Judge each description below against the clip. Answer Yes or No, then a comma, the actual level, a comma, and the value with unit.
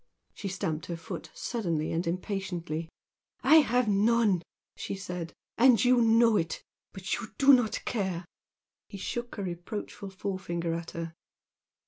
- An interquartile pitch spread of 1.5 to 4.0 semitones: No, average, 5.0 semitones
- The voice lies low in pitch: No, high, 195 Hz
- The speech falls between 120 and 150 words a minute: Yes, average, 140 wpm